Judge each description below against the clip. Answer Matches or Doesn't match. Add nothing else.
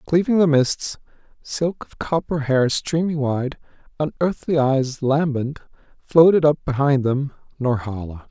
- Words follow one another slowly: Matches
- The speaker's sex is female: Doesn't match